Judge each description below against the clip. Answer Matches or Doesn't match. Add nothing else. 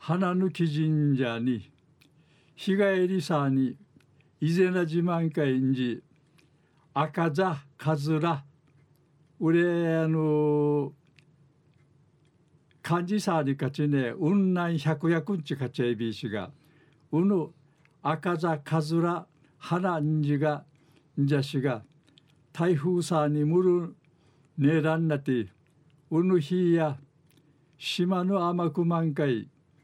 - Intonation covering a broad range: Doesn't match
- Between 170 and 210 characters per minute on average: Matches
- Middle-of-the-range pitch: Matches